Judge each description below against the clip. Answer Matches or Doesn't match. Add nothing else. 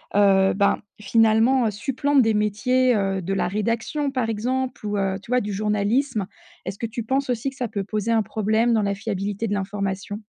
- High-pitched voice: Matches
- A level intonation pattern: Doesn't match